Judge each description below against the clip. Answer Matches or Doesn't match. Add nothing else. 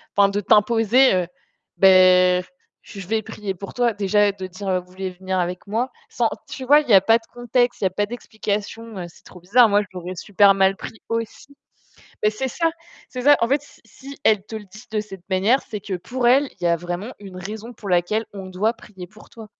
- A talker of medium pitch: Doesn't match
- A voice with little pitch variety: Doesn't match